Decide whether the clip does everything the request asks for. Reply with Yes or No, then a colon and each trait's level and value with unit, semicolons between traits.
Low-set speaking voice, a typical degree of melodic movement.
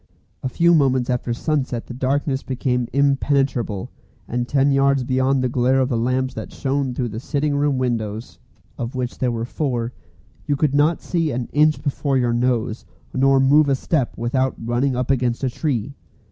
No: low, 130 Hz; narrow, 2.3 semitones